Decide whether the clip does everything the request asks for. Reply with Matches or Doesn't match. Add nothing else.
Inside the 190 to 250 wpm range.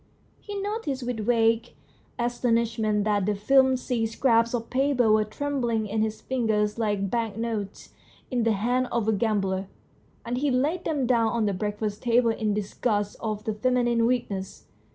Doesn't match